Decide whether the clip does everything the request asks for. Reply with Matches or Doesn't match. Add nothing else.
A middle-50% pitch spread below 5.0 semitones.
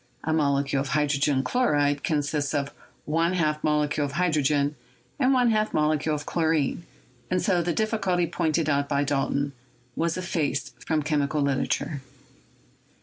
Matches